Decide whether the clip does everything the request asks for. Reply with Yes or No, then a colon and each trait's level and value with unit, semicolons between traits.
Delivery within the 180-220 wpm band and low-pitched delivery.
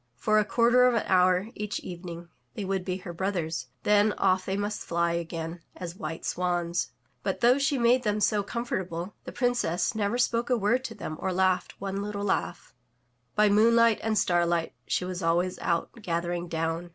No: average, 190 wpm; high, 190 Hz